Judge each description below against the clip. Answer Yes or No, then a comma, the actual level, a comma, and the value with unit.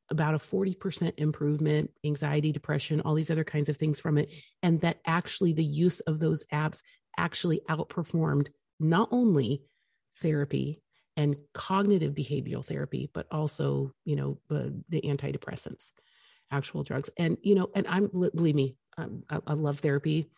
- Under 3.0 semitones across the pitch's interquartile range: Yes, narrow, 2.4 semitones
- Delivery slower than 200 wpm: Yes, average, 155 wpm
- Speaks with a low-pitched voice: No, medium, 155 Hz